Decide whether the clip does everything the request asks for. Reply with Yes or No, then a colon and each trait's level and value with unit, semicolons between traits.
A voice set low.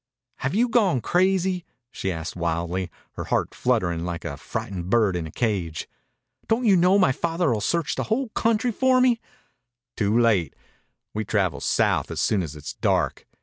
Yes: low, 115 Hz